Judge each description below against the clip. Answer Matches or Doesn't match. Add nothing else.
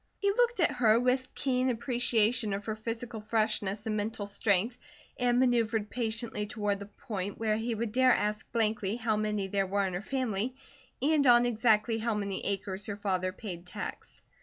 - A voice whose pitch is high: Matches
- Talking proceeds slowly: Doesn't match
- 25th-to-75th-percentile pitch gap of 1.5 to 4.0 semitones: Matches